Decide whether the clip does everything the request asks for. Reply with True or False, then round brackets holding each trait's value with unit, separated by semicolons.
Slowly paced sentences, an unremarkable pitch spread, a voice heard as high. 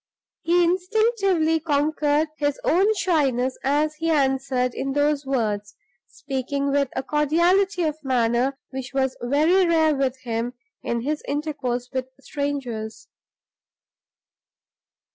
True (115 wpm; 3.4 semitones; 285 Hz)